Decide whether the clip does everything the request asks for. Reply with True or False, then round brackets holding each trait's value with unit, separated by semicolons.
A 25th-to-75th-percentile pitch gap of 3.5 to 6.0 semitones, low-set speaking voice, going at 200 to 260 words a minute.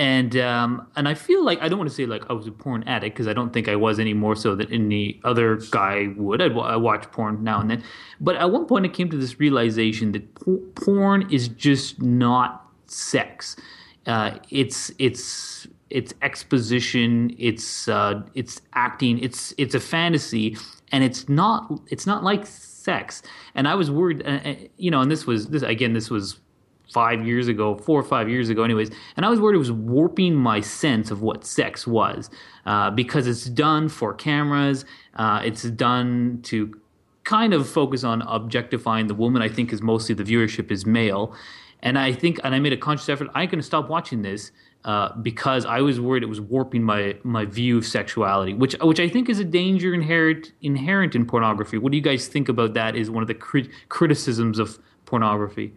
True (4.5 semitones; 120 Hz; 205 wpm)